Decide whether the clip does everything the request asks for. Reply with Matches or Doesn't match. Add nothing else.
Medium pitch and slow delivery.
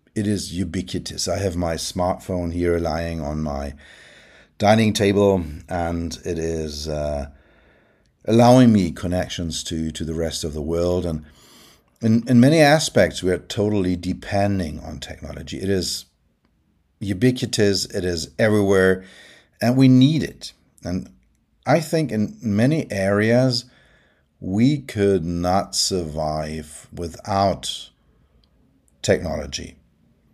Doesn't match